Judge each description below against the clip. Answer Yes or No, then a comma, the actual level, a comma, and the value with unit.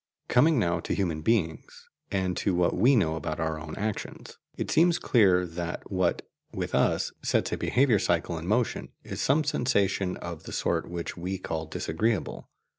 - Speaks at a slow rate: No, average, 175 wpm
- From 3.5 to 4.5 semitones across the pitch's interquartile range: No, average, 5.0 semitones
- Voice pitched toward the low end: Yes, very low, 90 Hz